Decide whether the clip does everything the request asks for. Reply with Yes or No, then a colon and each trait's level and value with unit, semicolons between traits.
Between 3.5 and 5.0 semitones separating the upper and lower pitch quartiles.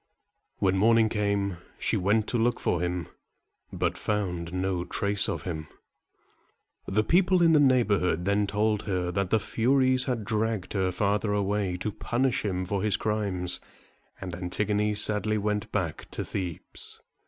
No: average, 2.9 semitones